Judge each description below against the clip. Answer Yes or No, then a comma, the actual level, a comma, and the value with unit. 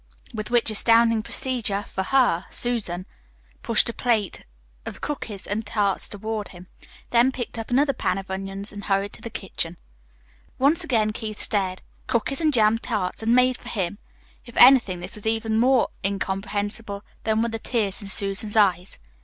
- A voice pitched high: Yes, high, 215 Hz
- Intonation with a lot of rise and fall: No, average, 3.1 semitones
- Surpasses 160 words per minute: Yes, average, 170 wpm